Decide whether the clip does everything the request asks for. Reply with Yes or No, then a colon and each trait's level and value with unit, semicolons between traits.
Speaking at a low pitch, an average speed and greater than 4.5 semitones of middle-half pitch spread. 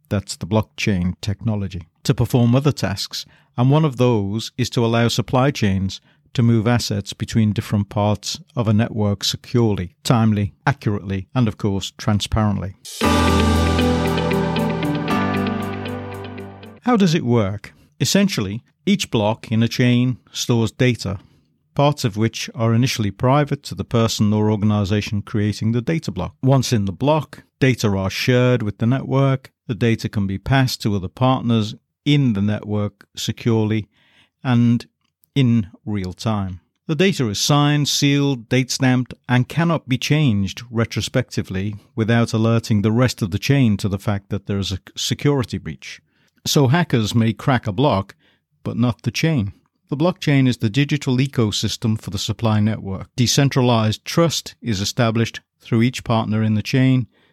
No: low, 115 Hz; average, 150 wpm; average, 3.8 semitones